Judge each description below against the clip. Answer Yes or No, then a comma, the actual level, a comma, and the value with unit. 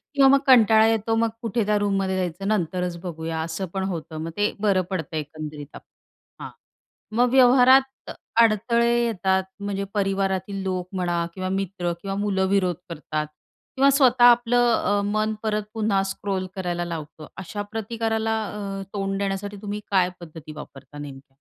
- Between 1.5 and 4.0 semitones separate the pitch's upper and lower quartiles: Yes, average, 3.7 semitones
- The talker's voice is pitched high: Yes, high, 195 Hz